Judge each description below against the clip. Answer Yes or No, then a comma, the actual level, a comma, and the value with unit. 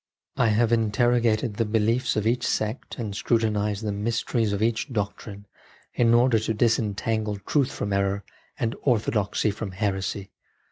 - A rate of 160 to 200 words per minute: No, average, 145 wpm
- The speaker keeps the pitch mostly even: Yes, narrow, 2.2 semitones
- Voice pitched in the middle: No, low, 110 Hz